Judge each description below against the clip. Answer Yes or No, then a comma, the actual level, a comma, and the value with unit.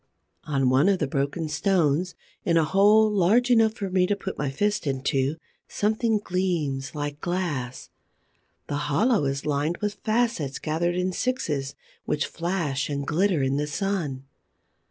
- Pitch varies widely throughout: Yes, wide, 5.8 semitones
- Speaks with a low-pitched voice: No, medium, 165 Hz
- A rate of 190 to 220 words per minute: No, average, 155 wpm